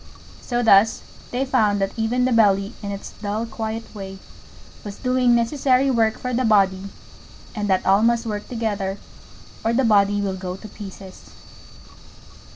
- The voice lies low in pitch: No, high, 220 Hz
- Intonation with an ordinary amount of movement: Yes, average, 3.0 semitones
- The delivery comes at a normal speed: Yes, average, 160 wpm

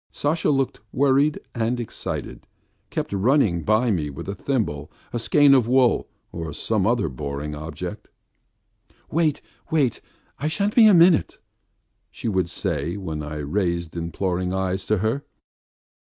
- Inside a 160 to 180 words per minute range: No, average, 140 wpm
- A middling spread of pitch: No, wide, 8.0 semitones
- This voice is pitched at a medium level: No, low, 105 Hz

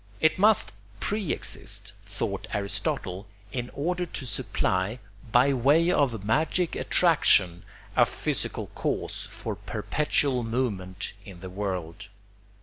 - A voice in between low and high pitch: No, low, 115 Hz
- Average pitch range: No, wide, 7.2 semitones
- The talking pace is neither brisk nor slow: No, slow, 115 wpm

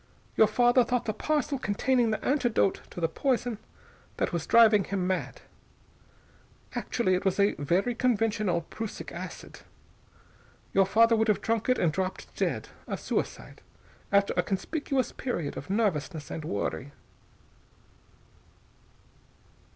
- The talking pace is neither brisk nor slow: No, slow, 130 wpm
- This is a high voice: Yes, high, 215 Hz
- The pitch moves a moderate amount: Yes, average, 4.6 semitones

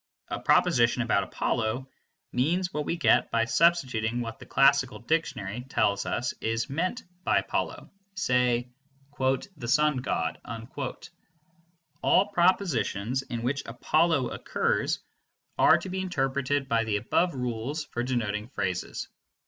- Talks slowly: Yes, slow, 125 wpm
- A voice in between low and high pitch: No, low, 130 Hz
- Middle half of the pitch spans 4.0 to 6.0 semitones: Yes, average, 5.0 semitones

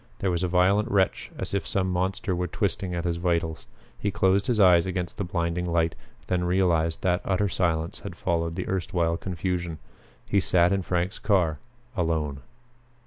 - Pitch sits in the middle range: No, very low, 90 Hz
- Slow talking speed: No, average, 175 wpm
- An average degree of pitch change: No, narrow, 2.0 semitones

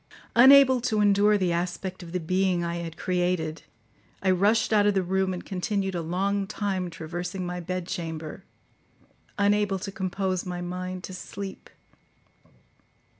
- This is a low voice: No, medium, 185 Hz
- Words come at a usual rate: Yes, average, 150 wpm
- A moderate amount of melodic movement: No, narrow, 2.2 semitones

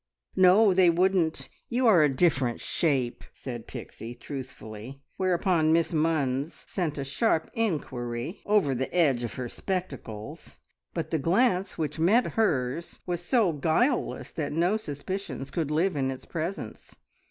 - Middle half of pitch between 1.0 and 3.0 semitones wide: No, wide, 5.6 semitones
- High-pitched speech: No, medium, 160 Hz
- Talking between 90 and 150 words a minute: Yes, average, 140 wpm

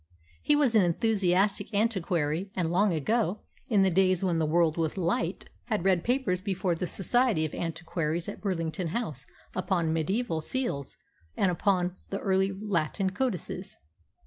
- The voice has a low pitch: No, medium, 185 Hz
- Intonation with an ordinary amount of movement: Yes, average, 3.5 semitones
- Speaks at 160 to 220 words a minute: No, average, 150 wpm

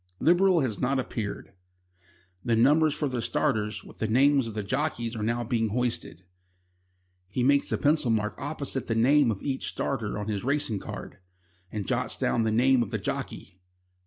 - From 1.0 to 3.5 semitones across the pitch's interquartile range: No, average, 4.3 semitones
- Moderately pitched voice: No, low, 120 Hz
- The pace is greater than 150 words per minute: Yes, average, 180 wpm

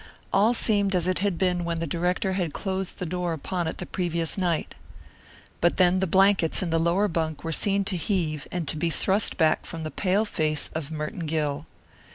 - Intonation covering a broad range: No, average, 2.9 semitones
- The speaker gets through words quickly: Yes, fast, 210 wpm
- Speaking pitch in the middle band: Yes, medium, 175 Hz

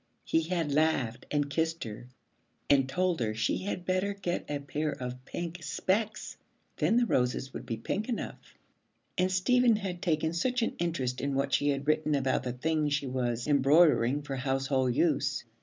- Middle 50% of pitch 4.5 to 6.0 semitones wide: Yes, average, 4.8 semitones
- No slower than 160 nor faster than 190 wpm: Yes, average, 175 wpm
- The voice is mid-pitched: Yes, medium, 145 Hz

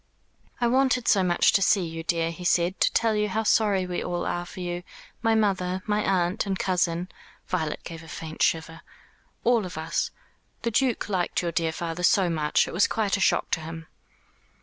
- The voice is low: No, medium, 180 Hz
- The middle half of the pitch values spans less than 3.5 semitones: No, average, 3.8 semitones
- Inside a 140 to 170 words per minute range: No, average, 200 wpm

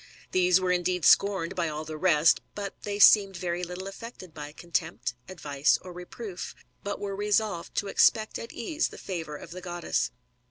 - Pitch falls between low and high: Yes, medium, 180 Hz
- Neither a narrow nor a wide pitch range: Yes, average, 3.0 semitones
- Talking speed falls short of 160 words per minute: No, average, 175 wpm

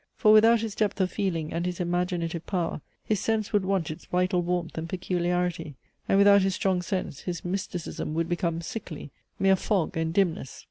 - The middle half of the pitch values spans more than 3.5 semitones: No, average, 2.7 semitones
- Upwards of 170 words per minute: Yes, average, 185 wpm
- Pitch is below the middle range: No, medium, 180 Hz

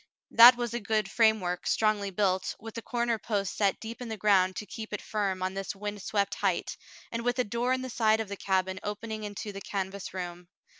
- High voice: Yes, high, 210 Hz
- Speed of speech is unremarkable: No, fast, 220 wpm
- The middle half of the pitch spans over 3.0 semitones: No, average, 2.7 semitones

